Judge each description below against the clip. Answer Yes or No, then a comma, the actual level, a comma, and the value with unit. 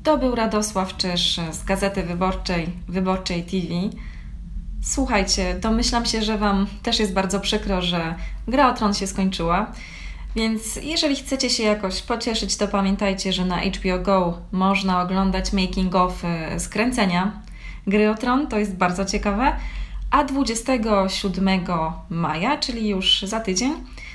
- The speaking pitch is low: No, high, 195 Hz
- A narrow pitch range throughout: No, average, 3.1 semitones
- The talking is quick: No, average, 135 wpm